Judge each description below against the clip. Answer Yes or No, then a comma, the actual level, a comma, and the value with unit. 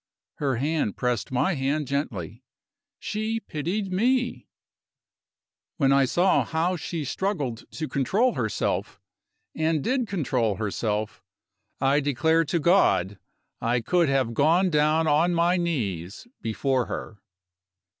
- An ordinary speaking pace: No, slow, 120 wpm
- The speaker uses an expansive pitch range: Yes, wide, 6.1 semitones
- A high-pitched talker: No, medium, 150 Hz